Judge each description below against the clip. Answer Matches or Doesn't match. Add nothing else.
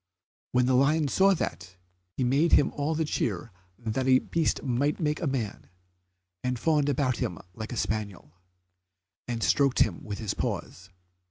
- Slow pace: Doesn't match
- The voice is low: Matches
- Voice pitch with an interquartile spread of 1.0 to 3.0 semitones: Doesn't match